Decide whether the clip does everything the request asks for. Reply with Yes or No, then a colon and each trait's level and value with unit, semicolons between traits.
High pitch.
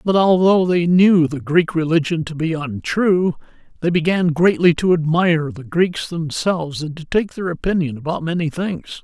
No: medium, 165 Hz